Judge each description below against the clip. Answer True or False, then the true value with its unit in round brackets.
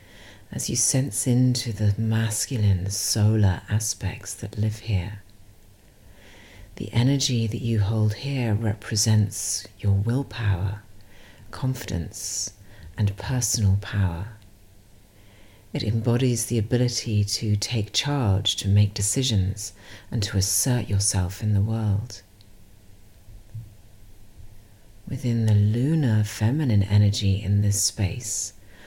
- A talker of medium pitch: False (105 Hz)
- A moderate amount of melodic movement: False (2.1 semitones)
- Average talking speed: False (100 wpm)